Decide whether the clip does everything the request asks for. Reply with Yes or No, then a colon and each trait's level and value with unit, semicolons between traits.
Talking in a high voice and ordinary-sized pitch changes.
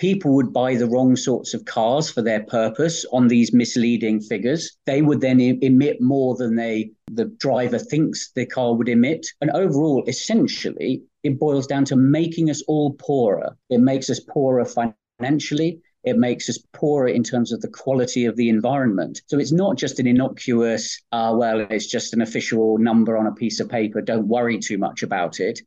No: low, 125 Hz; average, 3.1 semitones